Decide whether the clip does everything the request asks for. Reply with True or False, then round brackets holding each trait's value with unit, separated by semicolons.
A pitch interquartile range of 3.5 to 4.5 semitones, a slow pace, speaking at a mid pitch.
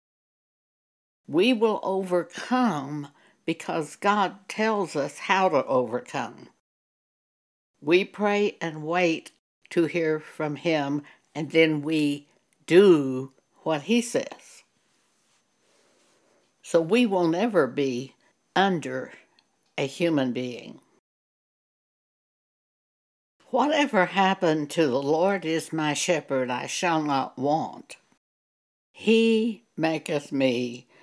False (5.1 semitones; 95 wpm; 160 Hz)